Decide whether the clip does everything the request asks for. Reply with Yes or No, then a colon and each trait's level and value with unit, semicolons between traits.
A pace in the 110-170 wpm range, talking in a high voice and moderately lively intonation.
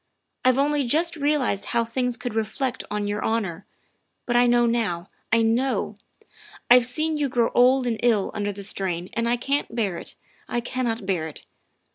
No: average, 185 wpm; high, 235 Hz; average, 3.5 semitones